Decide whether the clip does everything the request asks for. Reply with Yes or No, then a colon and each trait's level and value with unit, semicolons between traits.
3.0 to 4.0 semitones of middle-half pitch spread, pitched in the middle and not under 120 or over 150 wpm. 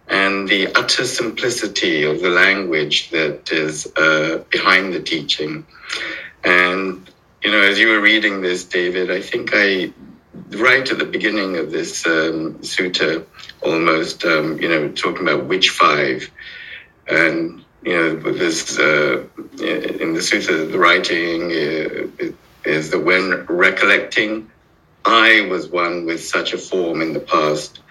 No: average, 3.3 semitones; very low, 90 Hz; average, 140 wpm